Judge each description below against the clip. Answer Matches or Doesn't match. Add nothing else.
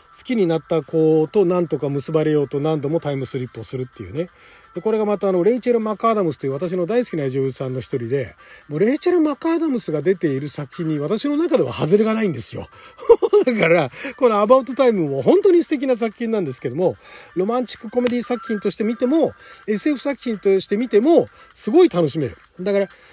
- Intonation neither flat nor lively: Doesn't match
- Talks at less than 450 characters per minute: Doesn't match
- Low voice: Doesn't match